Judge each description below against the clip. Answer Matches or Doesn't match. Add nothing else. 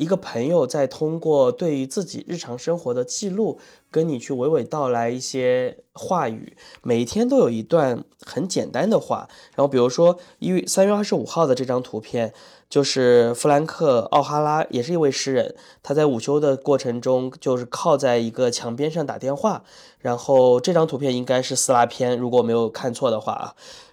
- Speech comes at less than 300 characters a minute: Matches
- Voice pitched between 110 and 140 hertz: Matches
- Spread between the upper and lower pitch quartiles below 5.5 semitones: Matches